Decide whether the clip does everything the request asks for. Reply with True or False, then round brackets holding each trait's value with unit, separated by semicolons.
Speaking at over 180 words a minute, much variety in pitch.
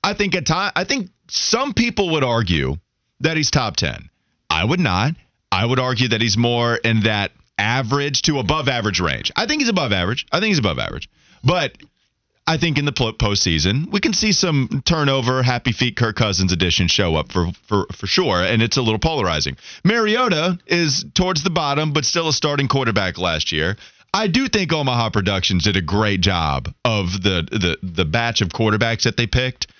True (195 wpm; 7.7 semitones)